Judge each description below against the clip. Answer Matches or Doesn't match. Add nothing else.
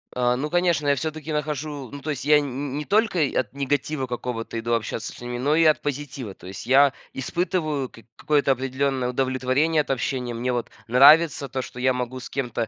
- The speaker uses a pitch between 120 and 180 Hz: Matches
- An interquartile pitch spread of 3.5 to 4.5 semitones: Doesn't match